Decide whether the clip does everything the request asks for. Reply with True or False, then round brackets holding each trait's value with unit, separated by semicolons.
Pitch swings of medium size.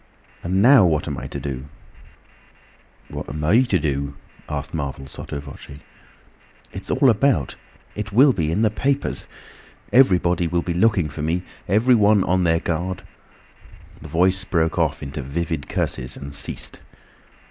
False (5.7 semitones)